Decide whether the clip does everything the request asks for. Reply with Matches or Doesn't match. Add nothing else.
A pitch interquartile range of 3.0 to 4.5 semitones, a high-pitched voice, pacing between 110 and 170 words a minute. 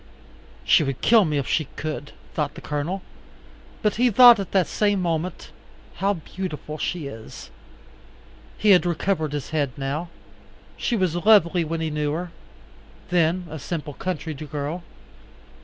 Doesn't match